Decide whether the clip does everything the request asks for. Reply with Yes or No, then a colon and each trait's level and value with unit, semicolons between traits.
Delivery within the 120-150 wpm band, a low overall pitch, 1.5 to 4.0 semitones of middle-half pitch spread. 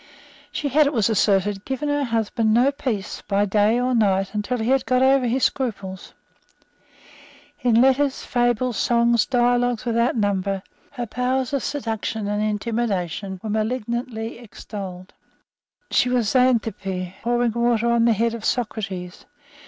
No: average, 145 wpm; high, 230 Hz; average, 3.2 semitones